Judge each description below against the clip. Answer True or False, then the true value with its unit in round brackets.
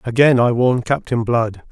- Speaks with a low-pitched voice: True (120 Hz)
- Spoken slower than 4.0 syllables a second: False (4.5 syllables/s)